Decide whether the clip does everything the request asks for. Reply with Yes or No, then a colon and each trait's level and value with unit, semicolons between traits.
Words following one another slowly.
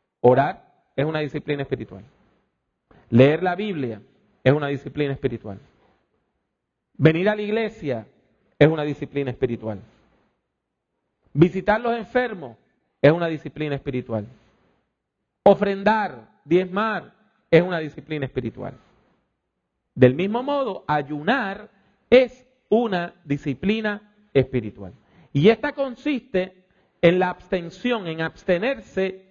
Yes: slow, 100 wpm